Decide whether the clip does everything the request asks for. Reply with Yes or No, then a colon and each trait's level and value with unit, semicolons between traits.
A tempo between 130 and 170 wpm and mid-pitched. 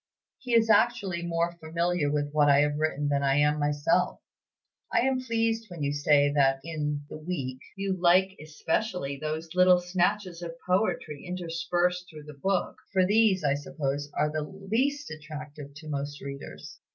Yes: average, 165 wpm; medium, 160 Hz